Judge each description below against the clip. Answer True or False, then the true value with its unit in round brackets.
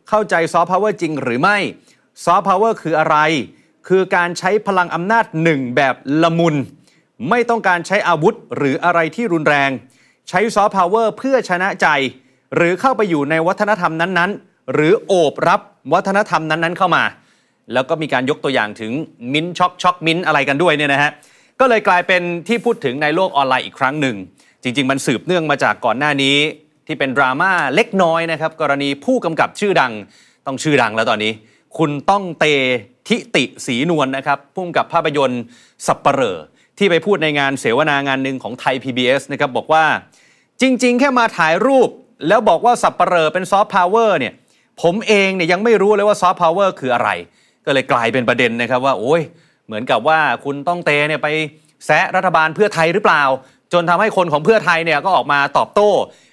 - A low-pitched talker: False (165 Hz)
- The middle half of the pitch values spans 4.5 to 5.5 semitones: True (5.2 semitones)